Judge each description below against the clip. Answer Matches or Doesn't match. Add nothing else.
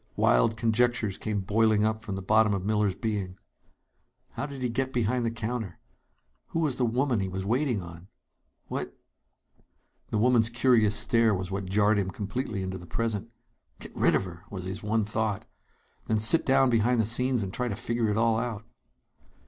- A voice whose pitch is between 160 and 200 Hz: Doesn't match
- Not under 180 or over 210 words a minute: Matches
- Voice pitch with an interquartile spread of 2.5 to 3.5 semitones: Matches